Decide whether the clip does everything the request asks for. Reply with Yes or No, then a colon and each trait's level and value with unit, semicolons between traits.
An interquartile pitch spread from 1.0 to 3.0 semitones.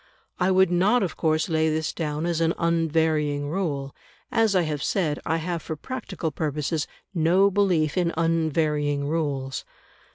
Yes: average, 2.7 semitones